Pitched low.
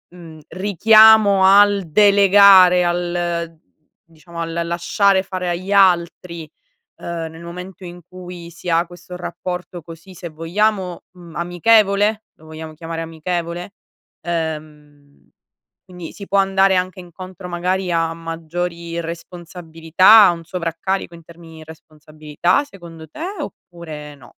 No: medium, 175 Hz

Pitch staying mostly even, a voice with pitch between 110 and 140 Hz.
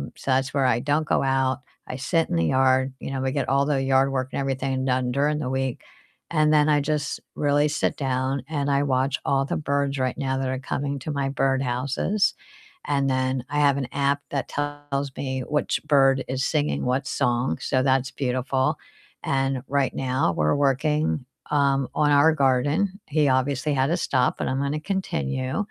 Yes: narrow, 1.7 semitones; low, 135 Hz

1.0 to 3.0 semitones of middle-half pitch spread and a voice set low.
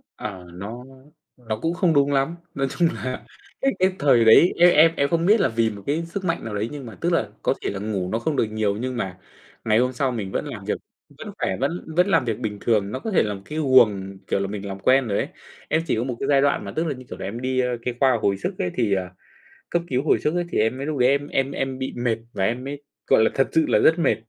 No: average, 5.1 semitones; low, 125 Hz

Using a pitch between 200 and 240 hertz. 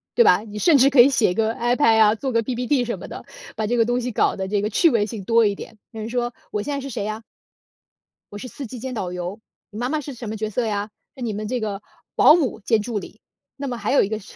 Yes: high, 230 Hz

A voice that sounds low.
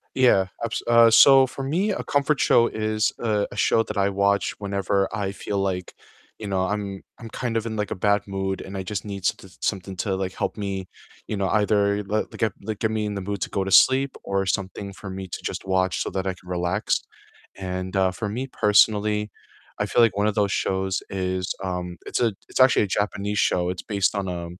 Yes: low, 100 Hz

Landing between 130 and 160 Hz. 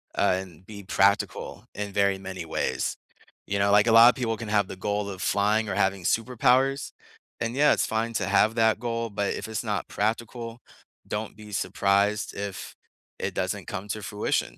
No: low, 105 Hz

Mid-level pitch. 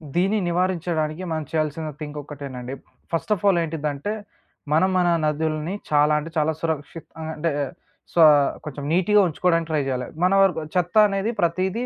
Yes: medium, 160 Hz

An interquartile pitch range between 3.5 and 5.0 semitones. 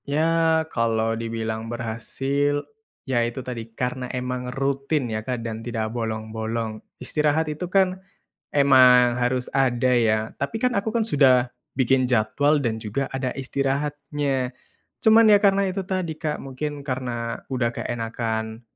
Yes: average, 4.1 semitones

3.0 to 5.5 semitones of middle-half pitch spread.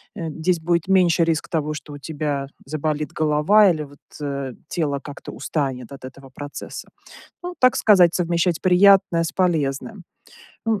Yes: average, 3.7 semitones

